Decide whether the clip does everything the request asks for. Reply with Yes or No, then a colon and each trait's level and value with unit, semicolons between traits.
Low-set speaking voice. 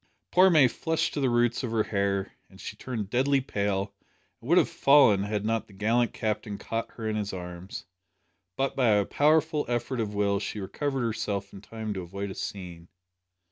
Yes: low, 110 Hz